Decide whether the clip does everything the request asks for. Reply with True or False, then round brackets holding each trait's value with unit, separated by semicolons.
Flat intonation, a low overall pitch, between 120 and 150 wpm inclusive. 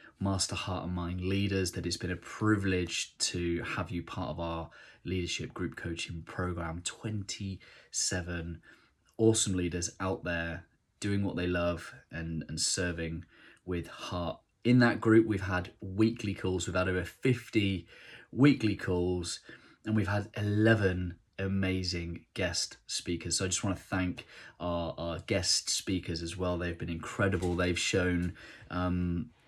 True (2.3 semitones; 90 Hz; 145 wpm)